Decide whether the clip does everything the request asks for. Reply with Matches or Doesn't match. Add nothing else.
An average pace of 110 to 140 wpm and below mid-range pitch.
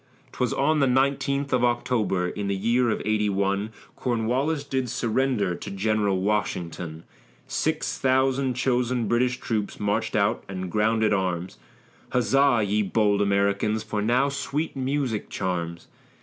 Matches